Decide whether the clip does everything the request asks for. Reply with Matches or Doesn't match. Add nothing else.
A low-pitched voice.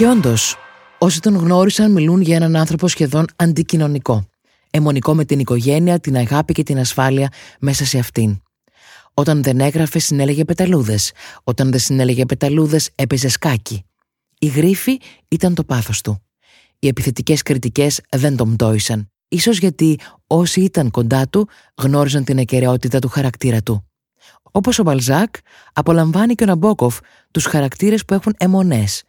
Doesn't match